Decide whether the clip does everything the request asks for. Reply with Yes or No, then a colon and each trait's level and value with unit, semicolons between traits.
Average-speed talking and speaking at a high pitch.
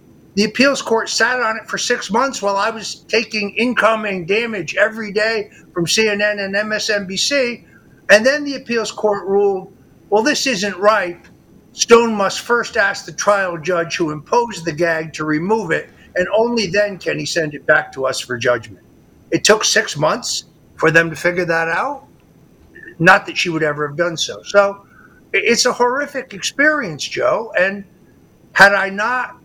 Yes: average, 175 wpm; high, 205 Hz